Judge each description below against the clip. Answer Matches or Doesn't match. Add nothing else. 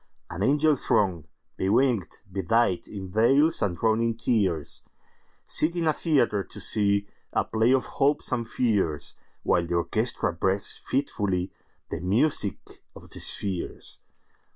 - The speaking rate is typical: Doesn't match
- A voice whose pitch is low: Matches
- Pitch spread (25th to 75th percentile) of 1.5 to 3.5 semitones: Doesn't match